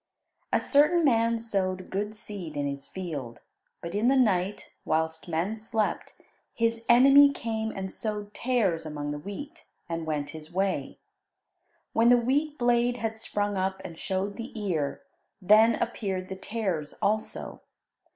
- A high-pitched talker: Yes, high, 205 Hz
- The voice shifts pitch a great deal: No, average, 4.8 semitones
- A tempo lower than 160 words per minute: Yes, average, 150 wpm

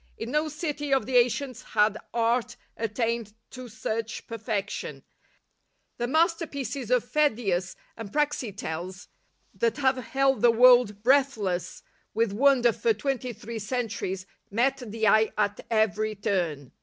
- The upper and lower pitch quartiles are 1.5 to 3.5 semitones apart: No, average, 4.2 semitones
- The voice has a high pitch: Yes, high, 235 Hz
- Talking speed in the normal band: No, slow, 130 wpm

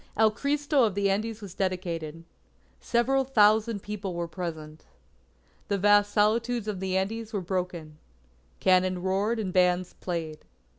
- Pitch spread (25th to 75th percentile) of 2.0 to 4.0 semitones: Yes, average, 3.3 semitones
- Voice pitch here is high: Yes, high, 195 Hz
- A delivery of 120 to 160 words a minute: Yes, average, 140 wpm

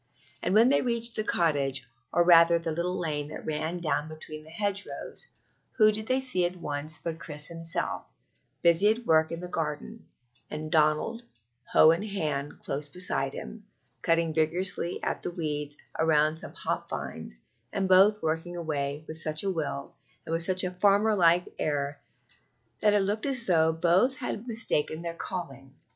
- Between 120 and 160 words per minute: No, average, 170 wpm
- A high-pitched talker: No, medium, 165 Hz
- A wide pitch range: No, average, 4.1 semitones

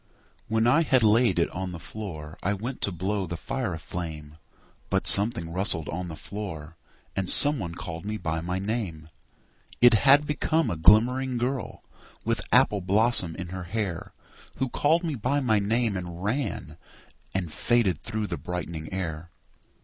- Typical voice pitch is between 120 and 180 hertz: No, low, 100 Hz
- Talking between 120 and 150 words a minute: No, average, 165 wpm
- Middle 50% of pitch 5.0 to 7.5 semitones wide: Yes, wide, 5.6 semitones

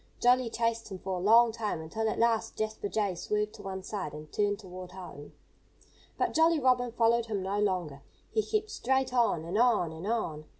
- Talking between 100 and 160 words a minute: No, average, 200 wpm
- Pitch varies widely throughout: No, average, 4.2 semitones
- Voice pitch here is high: Yes, high, 210 Hz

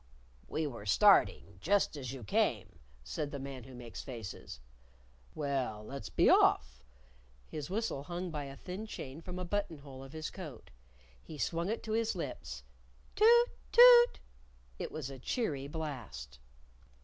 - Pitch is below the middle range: No, medium, 145 Hz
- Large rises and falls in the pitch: Yes, wide, 6.0 semitones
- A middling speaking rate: Yes, average, 155 wpm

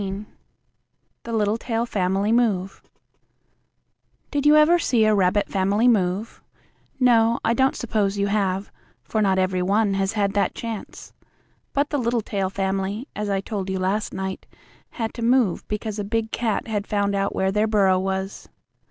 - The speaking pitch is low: No, high, 205 Hz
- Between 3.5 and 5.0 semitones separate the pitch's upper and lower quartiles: No, average, 2.9 semitones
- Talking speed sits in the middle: Yes, average, 160 wpm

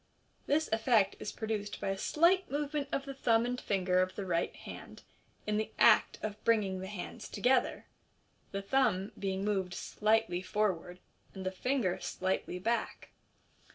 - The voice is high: Yes, high, 210 Hz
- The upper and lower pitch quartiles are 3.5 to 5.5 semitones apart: Yes, average, 4.4 semitones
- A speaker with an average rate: Yes, average, 160 wpm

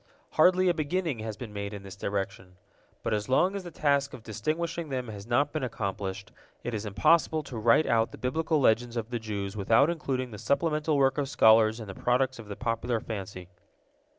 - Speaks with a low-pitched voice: Yes, low, 120 Hz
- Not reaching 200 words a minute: No, fast, 205 wpm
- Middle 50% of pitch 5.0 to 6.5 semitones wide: Yes, wide, 5.6 semitones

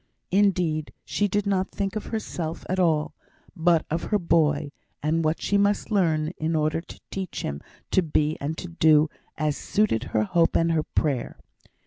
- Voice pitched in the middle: Yes, medium, 165 Hz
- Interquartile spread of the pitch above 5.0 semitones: No, average, 3.5 semitones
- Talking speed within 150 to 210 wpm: Yes, average, 175 wpm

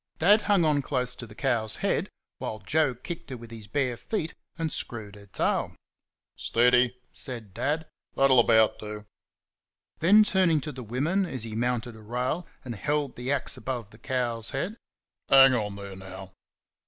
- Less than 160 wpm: No, average, 170 wpm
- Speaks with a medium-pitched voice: No, low, 125 Hz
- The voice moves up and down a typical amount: Yes, average, 4.9 semitones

